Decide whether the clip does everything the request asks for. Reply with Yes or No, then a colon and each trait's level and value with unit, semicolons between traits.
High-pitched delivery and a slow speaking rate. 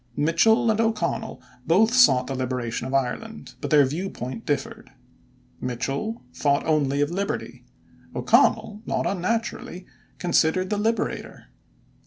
No: medium, 170 Hz; slow, 120 wpm